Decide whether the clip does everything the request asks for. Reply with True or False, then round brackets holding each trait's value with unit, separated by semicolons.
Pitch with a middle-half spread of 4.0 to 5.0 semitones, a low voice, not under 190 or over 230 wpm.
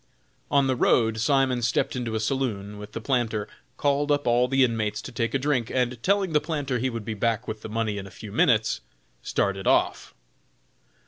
False (3.5 semitones; 120 Hz; 200 wpm)